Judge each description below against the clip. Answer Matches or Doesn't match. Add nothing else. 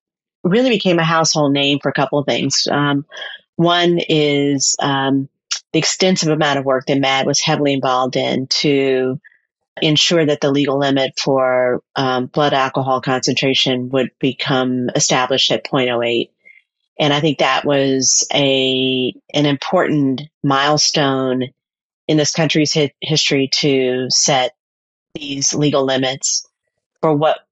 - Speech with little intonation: Matches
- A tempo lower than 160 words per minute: Matches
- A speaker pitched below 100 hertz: Doesn't match